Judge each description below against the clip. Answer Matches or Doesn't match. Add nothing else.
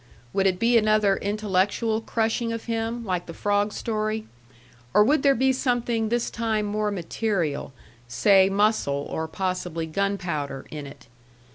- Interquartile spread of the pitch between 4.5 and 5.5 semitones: Doesn't match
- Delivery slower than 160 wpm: Matches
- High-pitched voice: Matches